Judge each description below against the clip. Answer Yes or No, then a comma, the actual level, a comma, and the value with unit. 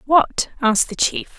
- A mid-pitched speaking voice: No, very high, 260 Hz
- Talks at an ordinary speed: Yes, average, 175 wpm